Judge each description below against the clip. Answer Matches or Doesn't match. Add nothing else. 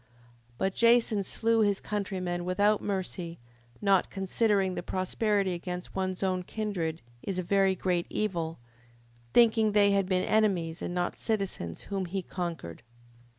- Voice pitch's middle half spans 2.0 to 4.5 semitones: Matches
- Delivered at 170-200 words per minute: Doesn't match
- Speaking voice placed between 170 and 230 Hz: Matches